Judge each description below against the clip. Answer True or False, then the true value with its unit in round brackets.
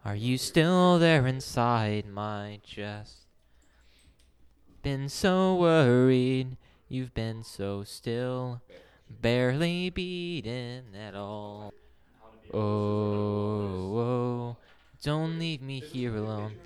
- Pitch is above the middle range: False (115 Hz)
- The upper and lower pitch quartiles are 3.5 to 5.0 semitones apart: True (4.1 semitones)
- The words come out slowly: True (90 wpm)